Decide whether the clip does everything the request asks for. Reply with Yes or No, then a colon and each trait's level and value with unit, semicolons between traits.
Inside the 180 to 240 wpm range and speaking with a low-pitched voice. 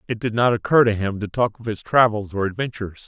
No: fast, 255 wpm; low, 110 Hz